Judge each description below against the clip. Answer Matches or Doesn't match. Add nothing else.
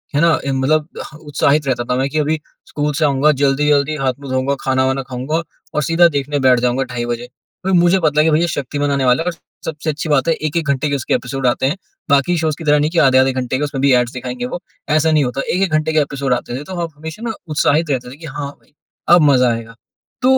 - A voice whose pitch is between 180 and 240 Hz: Doesn't match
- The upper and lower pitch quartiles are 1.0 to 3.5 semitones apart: Matches